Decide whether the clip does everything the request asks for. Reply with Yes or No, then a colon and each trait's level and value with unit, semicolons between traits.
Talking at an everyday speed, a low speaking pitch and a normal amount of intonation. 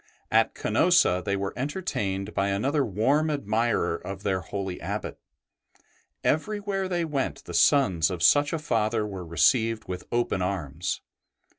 No: average, 145 wpm; low, 105 Hz; wide, 7.3 semitones